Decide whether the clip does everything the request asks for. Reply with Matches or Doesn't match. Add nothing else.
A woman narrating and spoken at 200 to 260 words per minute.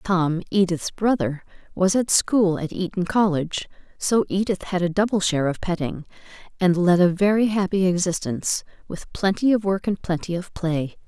Doesn't match